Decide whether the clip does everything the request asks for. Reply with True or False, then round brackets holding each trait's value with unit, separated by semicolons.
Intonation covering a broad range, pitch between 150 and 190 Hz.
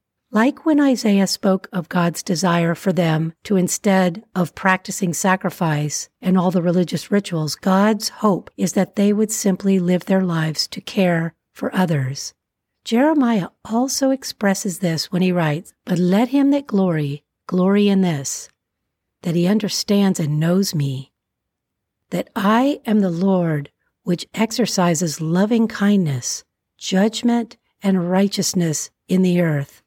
False (3.3 semitones; 185 Hz)